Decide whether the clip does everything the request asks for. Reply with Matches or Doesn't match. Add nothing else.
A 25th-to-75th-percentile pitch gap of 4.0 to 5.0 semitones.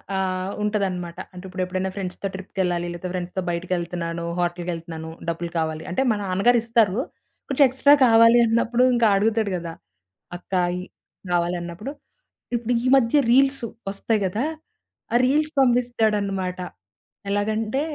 Matches